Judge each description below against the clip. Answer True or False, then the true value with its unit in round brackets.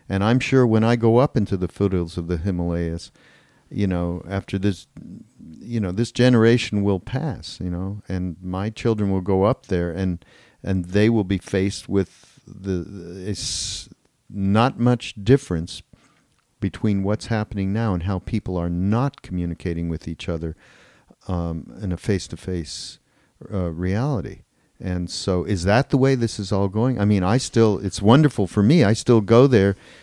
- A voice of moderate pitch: False (100 Hz)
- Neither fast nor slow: True (170 wpm)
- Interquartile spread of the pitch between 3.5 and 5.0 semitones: True (3.9 semitones)